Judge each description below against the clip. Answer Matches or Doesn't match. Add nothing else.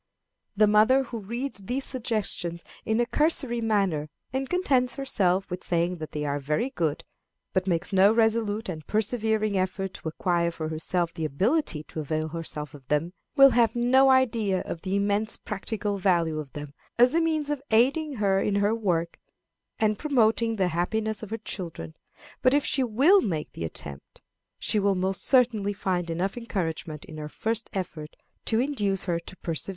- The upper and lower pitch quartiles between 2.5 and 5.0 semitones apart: Doesn't match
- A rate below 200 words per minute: Matches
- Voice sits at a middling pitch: Doesn't match